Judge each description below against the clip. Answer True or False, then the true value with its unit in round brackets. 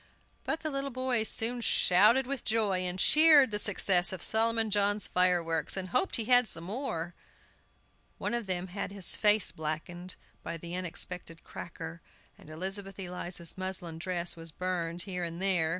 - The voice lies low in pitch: False (185 Hz)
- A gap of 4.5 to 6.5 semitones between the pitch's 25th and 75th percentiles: False (4.1 semitones)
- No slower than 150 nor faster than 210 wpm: True (165 wpm)